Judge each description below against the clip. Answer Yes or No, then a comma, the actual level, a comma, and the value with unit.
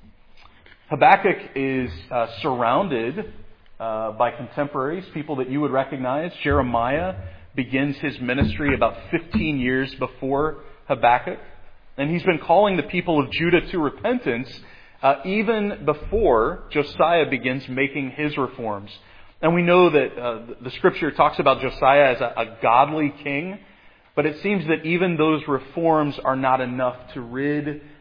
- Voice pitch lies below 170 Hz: Yes, medium, 140 Hz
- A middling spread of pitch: Yes, average, 3.5 semitones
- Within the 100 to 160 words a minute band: Yes, average, 140 wpm